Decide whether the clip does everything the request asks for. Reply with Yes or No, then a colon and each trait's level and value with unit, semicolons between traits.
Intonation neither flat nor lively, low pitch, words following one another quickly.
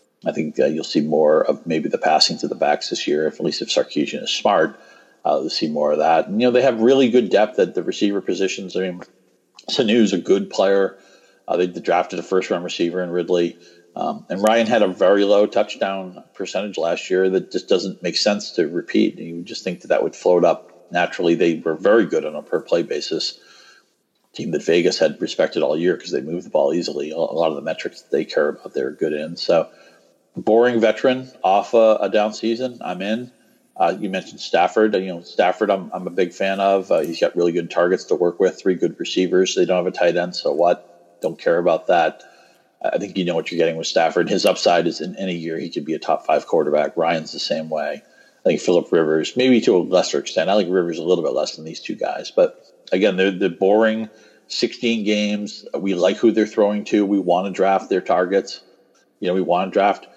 Yes: average, 4.2 semitones; low, 100 Hz; fast, 235 wpm